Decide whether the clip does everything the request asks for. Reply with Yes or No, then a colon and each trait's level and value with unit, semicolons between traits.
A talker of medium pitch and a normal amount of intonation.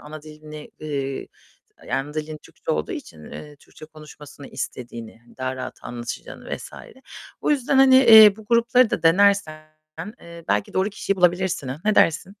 No: medium, 155 Hz; wide, 6.5 semitones